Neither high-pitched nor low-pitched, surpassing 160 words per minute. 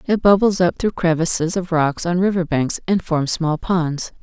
Yes: medium, 170 Hz; average, 200 wpm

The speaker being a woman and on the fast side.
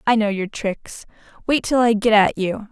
Yes: female; fast, 220 wpm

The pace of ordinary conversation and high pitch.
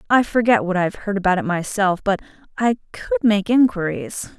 Yes: average, 190 wpm; high, 200 Hz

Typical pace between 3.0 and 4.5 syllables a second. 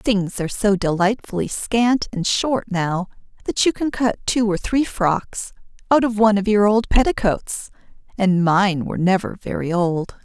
Yes: 4.4 syllables/s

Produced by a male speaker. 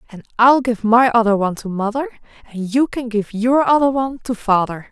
No: female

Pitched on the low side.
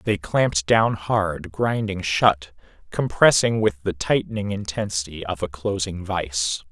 Yes: very low, 95 Hz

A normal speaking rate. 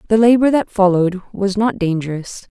Yes: average, 165 wpm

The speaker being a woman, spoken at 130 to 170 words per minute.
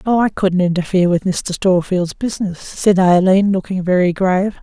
Yes: female; average, 155 wpm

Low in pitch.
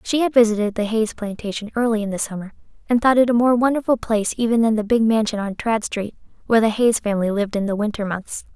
No: high, 220 Hz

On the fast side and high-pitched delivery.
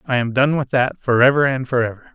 No: fast, 225 wpm; low, 125 Hz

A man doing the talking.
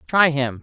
No: female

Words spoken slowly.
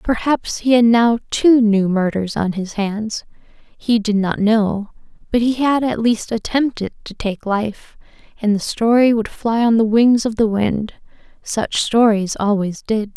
No: average, 175 wpm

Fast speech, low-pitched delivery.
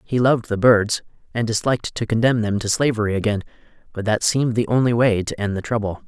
Yes: fast, 215 wpm; low, 110 Hz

